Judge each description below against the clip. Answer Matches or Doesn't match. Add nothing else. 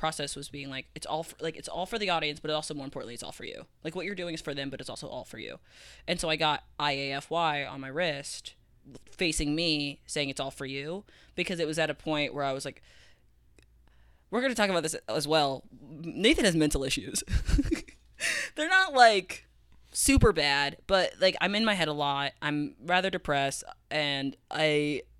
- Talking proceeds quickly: Matches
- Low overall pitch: Doesn't match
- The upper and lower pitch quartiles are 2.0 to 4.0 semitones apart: Matches